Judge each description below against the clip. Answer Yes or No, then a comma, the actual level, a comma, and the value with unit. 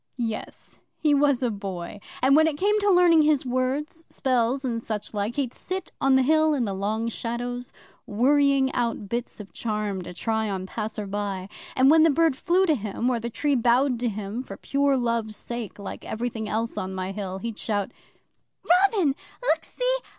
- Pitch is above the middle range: Yes, high, 240 Hz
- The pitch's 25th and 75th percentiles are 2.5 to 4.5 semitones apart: No, average, 5.1 semitones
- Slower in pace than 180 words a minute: No, average, 185 wpm